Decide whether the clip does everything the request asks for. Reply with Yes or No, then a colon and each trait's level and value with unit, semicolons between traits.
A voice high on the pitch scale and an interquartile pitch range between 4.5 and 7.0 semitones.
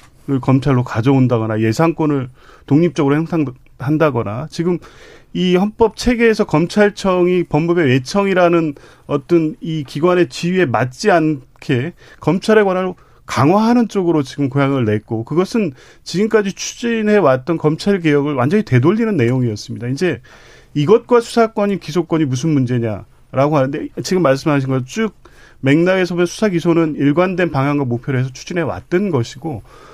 No: medium, 155 Hz; wide, 5.4 semitones